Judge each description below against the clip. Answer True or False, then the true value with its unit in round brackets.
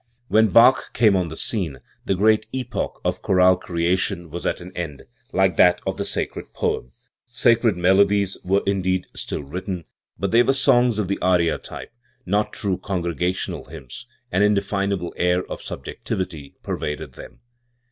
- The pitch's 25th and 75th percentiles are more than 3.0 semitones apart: False (2.7 semitones)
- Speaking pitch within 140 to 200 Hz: False (95 Hz)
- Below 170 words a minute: True (160 wpm)